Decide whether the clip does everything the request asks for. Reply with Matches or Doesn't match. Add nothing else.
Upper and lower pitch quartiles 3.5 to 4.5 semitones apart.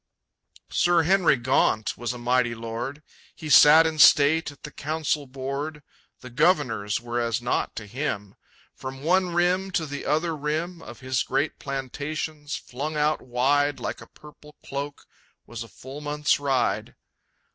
Matches